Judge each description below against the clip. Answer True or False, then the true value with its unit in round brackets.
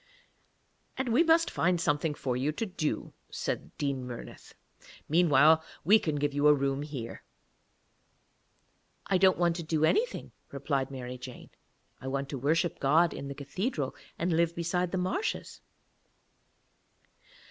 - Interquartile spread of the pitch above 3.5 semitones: True (4.3 semitones)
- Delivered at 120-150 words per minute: True (145 wpm)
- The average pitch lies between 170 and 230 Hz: False (155 Hz)